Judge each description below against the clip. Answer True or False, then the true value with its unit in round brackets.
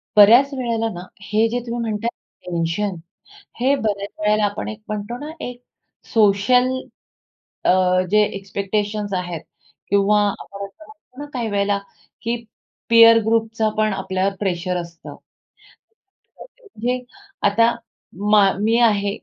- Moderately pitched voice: False (210 Hz)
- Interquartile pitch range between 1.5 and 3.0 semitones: True (2.6 semitones)